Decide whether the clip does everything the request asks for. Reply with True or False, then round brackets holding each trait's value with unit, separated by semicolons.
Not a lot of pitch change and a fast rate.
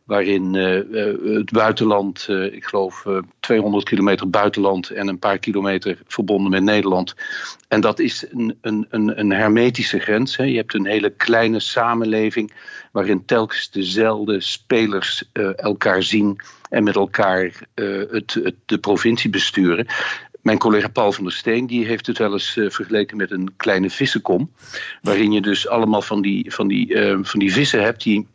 False (2.2 semitones; 170 wpm)